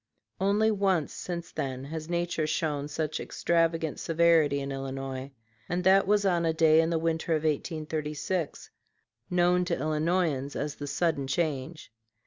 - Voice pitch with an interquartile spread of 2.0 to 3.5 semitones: Yes, average, 2.9 semitones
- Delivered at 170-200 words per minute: No, average, 145 wpm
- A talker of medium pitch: Yes, medium, 160 Hz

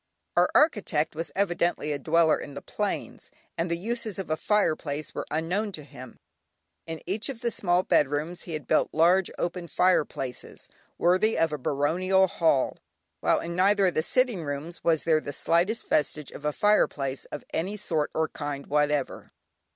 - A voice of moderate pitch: Yes, medium, 165 Hz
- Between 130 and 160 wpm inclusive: No, average, 175 wpm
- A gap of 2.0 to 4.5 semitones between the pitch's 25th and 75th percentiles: Yes, average, 4.1 semitones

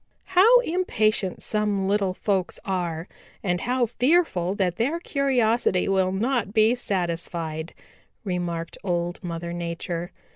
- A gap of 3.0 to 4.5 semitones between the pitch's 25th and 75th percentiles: No, average, 5.3 semitones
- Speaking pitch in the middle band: No, high, 195 Hz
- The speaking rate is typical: No, slow, 115 wpm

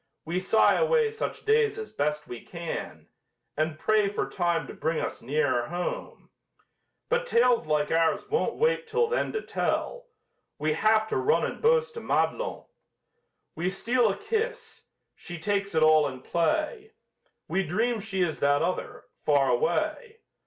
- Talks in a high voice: Yes, high, 205 Hz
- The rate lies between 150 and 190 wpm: Yes, average, 160 wpm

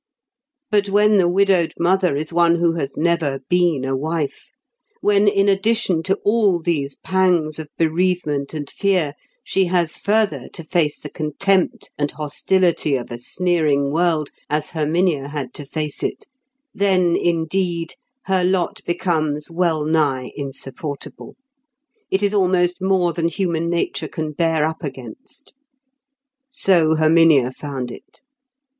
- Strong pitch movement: No, average, 3.8 semitones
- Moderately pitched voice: Yes, medium, 170 Hz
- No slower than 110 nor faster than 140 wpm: Yes, slow, 135 wpm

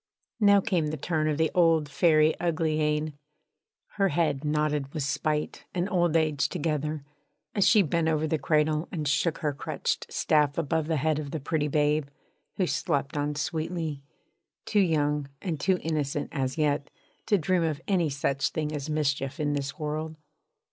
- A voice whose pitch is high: No, medium, 155 Hz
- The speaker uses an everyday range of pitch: No, narrow, 1.8 semitones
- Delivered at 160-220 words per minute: Yes, average, 170 wpm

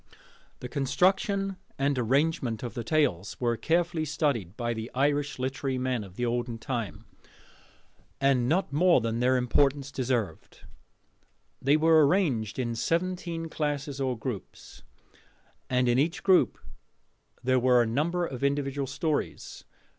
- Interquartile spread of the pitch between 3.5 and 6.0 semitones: Yes, average, 4.1 semitones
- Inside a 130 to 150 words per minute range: Yes, slow, 135 wpm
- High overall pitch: No, low, 135 Hz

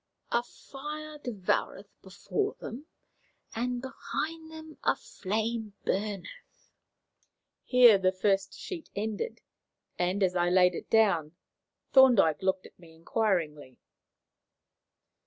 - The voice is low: No, high, 210 Hz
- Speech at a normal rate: No, slow, 105 wpm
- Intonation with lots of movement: Yes, wide, 6.1 semitones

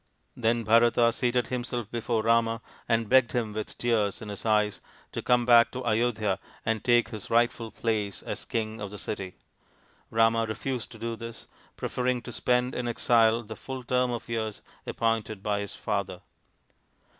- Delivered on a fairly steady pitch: Yes, narrow, 1.8 semitones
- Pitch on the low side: Yes, low, 115 Hz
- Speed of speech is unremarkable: Yes, average, 165 wpm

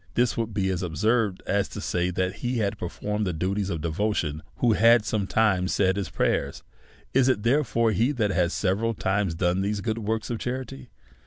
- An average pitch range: Yes, average, 3.6 semitones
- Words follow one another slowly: No, average, 190 wpm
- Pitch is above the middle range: No, low, 105 Hz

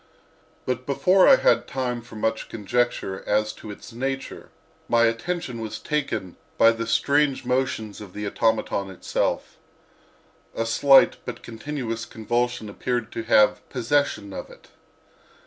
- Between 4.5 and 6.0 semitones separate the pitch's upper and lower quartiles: No, average, 3.3 semitones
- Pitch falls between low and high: No, low, 115 Hz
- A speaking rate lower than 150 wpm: Yes, slow, 135 wpm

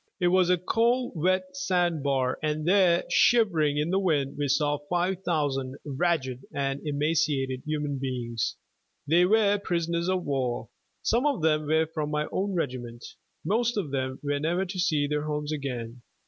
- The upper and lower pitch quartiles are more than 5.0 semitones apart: No, average, 4.4 semitones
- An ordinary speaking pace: Yes, average, 160 wpm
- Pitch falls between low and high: Yes, medium, 155 Hz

